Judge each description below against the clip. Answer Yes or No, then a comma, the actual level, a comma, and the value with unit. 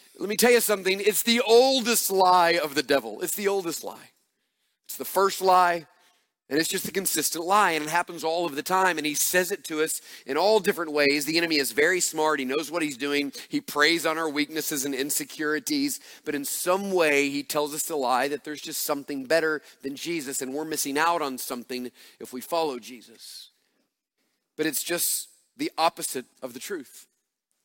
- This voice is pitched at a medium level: Yes, medium, 160 Hz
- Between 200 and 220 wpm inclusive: Yes, fast, 205 wpm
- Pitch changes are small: No, average, 4.0 semitones